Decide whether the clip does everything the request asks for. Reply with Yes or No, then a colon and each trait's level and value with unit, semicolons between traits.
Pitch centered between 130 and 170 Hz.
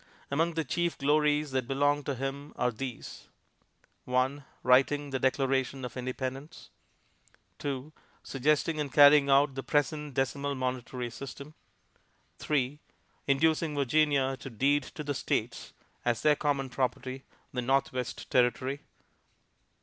Yes: low, 135 Hz